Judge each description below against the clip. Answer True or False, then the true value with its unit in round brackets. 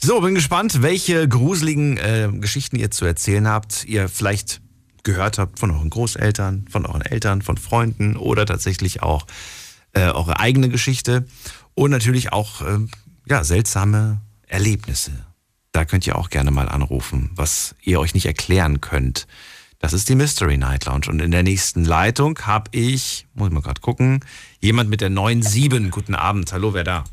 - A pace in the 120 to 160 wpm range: False (170 wpm)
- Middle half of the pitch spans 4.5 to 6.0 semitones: True (5.3 semitones)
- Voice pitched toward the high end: False (105 Hz)